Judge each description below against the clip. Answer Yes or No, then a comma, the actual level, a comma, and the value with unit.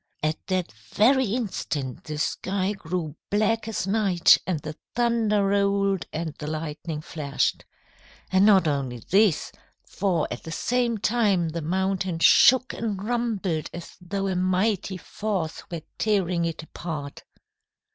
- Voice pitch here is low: No, medium, 185 Hz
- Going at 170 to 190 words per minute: No, slow, 135 wpm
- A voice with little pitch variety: No, average, 4.4 semitones